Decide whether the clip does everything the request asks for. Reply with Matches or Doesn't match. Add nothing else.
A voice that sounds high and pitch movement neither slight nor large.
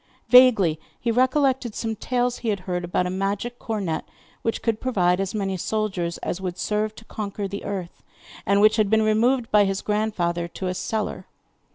Matches